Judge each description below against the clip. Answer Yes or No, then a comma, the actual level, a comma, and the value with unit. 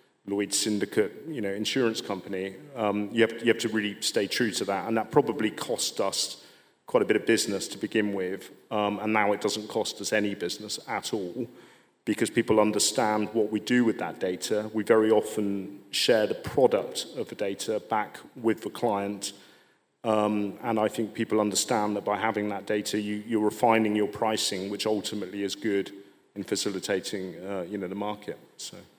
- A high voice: No, low, 105 Hz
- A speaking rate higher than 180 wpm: Yes, average, 190 wpm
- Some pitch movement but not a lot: No, narrow, 1.4 semitones